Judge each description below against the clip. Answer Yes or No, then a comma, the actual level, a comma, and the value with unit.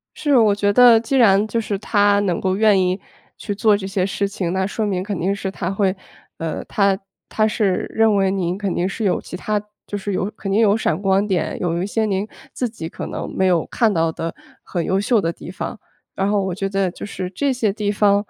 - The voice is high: Yes, high, 200 Hz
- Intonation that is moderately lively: No, narrow, 2.0 semitones